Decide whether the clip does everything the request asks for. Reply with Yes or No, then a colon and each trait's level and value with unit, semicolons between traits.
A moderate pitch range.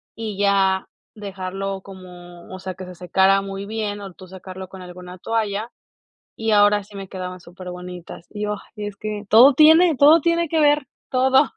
Yes: average, 3.1 semitones